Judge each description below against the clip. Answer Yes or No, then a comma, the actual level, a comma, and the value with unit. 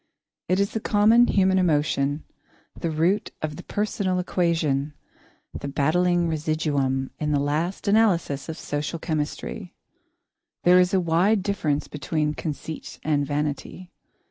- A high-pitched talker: No, medium, 160 Hz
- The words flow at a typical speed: No, slow, 130 wpm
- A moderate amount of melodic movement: Yes, average, 3.8 semitones